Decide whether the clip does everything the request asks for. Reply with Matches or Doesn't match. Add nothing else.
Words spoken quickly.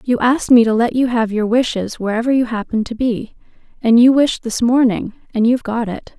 Matches